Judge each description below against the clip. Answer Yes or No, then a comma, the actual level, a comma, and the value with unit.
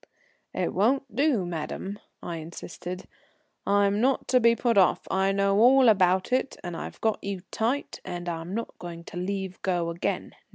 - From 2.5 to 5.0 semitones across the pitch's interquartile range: Yes, average, 4.6 semitones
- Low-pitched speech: No, high, 195 Hz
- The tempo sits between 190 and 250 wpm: No, average, 170 wpm